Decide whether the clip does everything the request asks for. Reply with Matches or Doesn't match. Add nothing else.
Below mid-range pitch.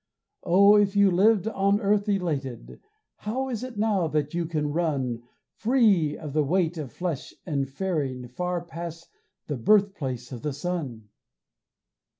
Doesn't match